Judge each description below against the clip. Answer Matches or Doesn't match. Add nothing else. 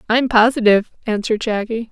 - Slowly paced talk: Matches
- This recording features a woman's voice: Matches